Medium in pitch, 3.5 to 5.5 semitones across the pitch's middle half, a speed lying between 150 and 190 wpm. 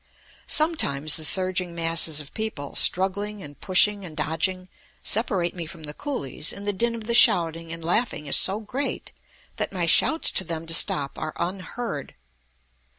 Yes: medium, 180 Hz; average, 4.6 semitones; average, 165 wpm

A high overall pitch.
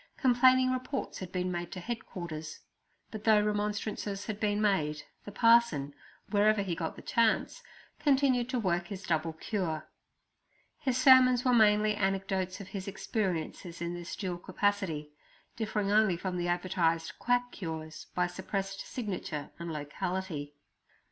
Yes: high, 195 Hz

